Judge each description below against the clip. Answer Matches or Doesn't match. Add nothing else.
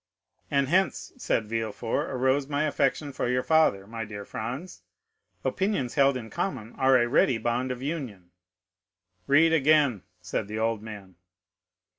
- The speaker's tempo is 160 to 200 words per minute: Doesn't match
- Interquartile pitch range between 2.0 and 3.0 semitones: Doesn't match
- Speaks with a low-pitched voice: Matches